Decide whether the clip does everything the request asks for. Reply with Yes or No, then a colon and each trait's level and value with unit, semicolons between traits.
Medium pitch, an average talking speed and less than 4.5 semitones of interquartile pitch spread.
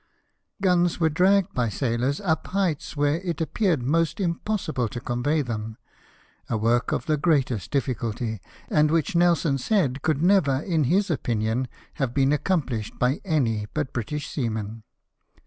No: medium, 145 Hz; average, 160 wpm; wide, 5.6 semitones